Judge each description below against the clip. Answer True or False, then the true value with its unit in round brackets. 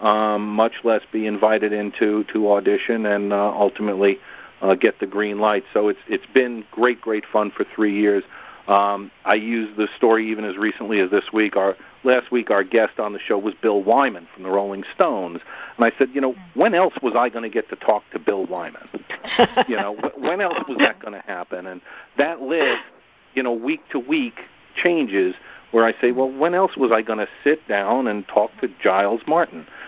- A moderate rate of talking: False (210 wpm)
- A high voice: False (110 Hz)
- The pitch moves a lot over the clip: False (3.8 semitones)